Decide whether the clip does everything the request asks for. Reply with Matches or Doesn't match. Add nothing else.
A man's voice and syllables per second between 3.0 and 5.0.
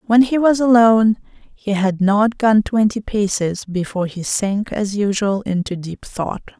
Doesn't match